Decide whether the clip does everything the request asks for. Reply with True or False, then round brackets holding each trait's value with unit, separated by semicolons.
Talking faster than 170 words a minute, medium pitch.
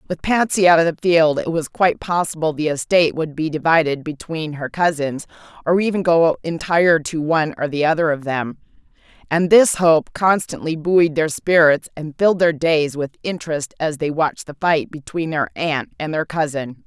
True (190 wpm; 160 Hz)